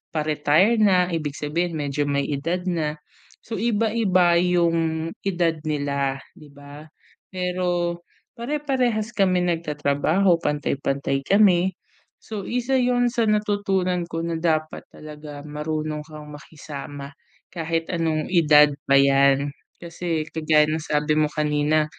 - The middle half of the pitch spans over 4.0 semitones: No, average, 3.6 semitones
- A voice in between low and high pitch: Yes, medium, 165 Hz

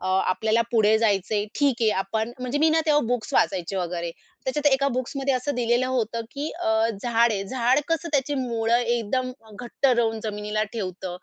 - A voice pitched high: Yes, high, 235 Hz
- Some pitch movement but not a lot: Yes, average, 3.5 semitones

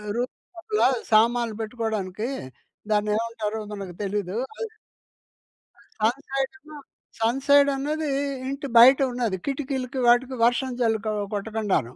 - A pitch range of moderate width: Yes, average, 4.0 semitones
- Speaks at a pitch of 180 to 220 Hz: No, high, 240 Hz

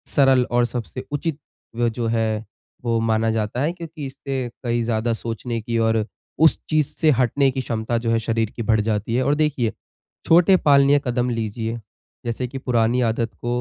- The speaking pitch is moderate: No, low, 120 Hz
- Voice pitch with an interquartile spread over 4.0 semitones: No, average, 3.0 semitones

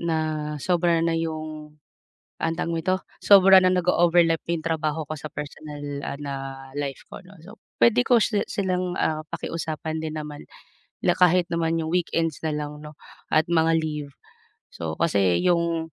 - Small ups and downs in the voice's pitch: Yes, narrow, 2.2 semitones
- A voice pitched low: No, medium, 165 Hz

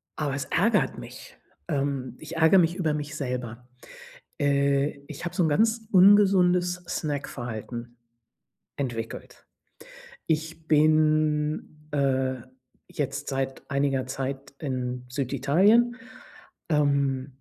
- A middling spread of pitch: Yes, average, 3.1 semitones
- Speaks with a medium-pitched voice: Yes, medium, 145 Hz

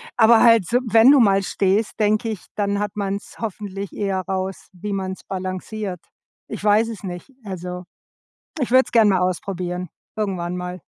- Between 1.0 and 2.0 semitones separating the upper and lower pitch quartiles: No, average, 2.7 semitones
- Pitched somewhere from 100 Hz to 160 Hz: No, high, 195 Hz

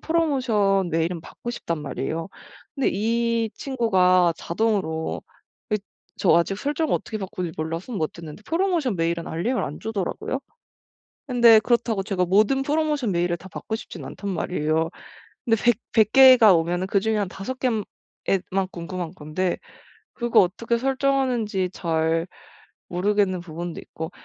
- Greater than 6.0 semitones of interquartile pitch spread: No, wide, 5.6 semitones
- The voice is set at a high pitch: Yes, high, 195 Hz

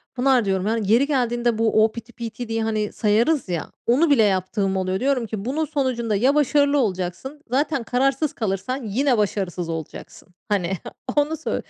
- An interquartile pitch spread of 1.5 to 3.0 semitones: No, average, 5.0 semitones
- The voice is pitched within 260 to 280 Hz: No, high, 230 Hz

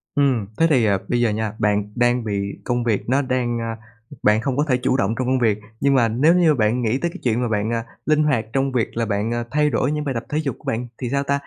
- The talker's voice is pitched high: No, low, 120 Hz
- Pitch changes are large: No, average, 3.6 semitones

